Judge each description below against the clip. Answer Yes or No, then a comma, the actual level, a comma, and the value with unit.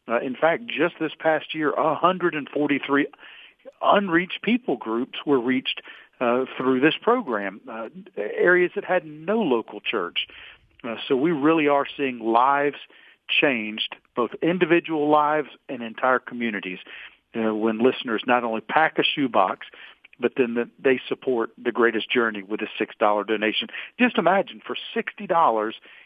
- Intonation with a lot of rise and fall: Yes, wide, 6.2 semitones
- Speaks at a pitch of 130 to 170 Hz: Yes, medium, 140 Hz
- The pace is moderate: Yes, average, 145 wpm